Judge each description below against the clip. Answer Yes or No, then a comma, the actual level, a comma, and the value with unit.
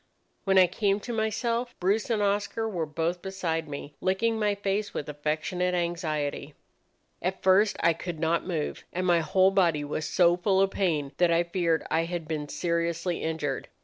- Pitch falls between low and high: Yes, medium, 175 Hz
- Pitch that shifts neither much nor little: Yes, average, 3.3 semitones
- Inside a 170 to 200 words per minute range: Yes, average, 180 wpm